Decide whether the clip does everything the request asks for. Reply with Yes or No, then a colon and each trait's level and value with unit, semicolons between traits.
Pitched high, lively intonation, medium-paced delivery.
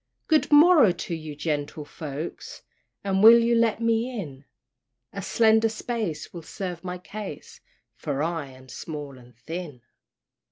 No: medium, 175 Hz; wide, 7.2 semitones; average, 145 wpm